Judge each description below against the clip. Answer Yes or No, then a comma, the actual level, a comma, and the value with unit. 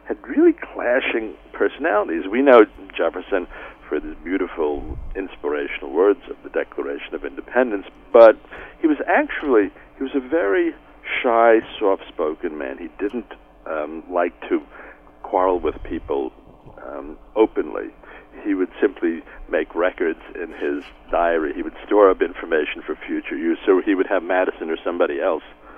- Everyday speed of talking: Yes, average, 145 wpm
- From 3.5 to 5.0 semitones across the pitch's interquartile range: Yes, average, 4.2 semitones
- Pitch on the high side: Yes, very high, 350 Hz